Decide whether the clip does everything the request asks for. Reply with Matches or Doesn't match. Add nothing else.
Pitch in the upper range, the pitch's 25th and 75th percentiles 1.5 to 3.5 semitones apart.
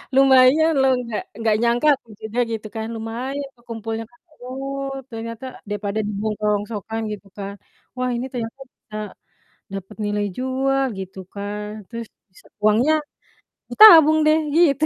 Doesn't match